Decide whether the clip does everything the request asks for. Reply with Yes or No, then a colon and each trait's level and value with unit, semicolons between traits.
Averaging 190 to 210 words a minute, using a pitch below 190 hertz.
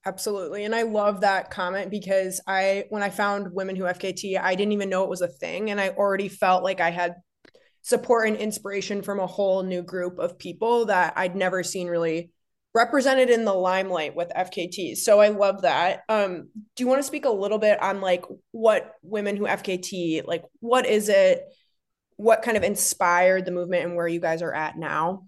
No: fast, 205 wpm; high, 195 Hz